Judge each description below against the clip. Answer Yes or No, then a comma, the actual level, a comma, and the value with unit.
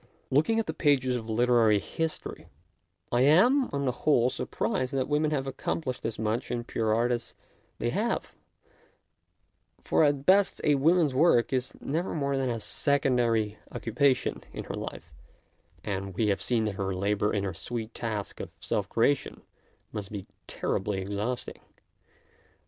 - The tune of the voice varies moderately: Yes, average, 4.6 semitones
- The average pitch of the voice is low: Yes, low, 125 Hz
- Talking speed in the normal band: Yes, average, 155 wpm